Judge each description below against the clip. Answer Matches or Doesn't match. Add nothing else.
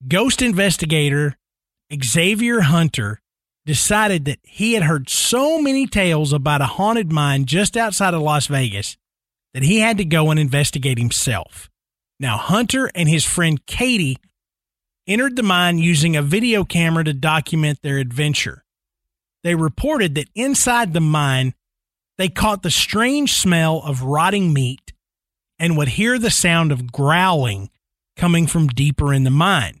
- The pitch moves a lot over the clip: Matches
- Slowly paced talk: Doesn't match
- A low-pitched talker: Doesn't match